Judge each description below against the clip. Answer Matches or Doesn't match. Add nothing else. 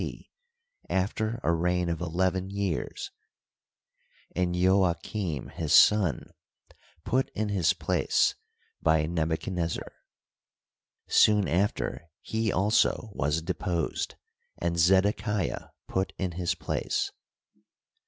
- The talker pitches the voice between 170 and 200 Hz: Doesn't match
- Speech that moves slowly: Matches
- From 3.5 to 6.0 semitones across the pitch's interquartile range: Doesn't match